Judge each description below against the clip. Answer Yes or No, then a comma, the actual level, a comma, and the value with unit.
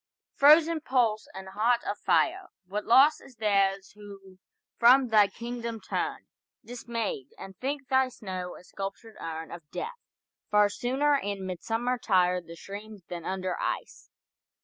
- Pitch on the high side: Yes, high, 215 Hz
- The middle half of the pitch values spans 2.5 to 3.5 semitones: No, average, 4.6 semitones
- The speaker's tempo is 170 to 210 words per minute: No, average, 145 wpm